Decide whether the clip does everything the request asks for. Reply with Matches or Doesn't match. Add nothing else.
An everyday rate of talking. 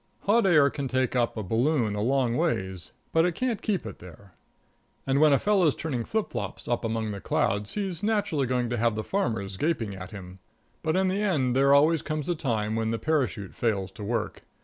Doesn't match